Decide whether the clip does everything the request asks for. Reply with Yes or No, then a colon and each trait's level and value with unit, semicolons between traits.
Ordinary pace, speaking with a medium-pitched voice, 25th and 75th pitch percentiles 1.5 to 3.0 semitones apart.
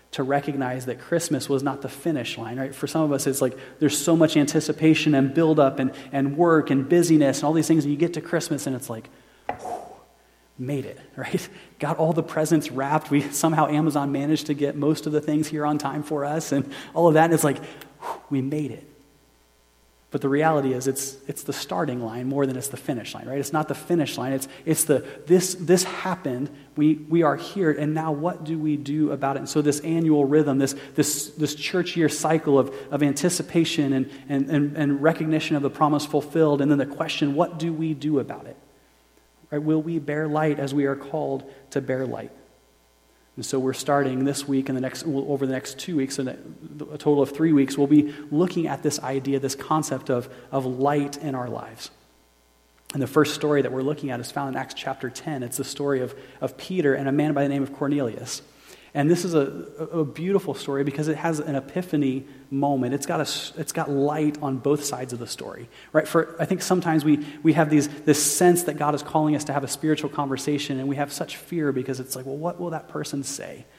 No: fast, 230 wpm; medium, 145 Hz; narrow, 2.4 semitones